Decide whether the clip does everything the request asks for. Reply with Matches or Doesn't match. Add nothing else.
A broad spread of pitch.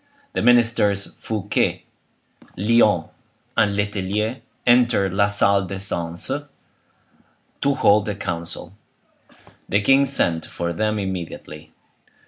Doesn't match